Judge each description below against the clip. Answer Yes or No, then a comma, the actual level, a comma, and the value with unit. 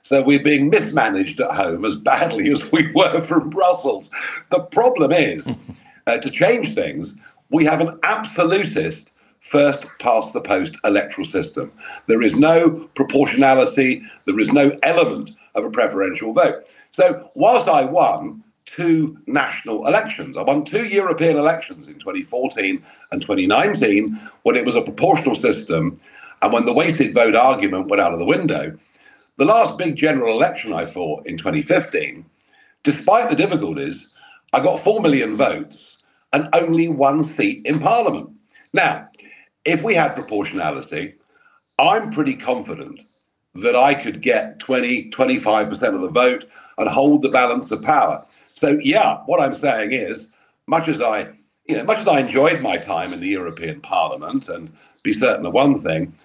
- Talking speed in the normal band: Yes, average, 160 wpm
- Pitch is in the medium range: Yes, medium, 165 Hz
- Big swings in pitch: Yes, wide, 9.0 semitones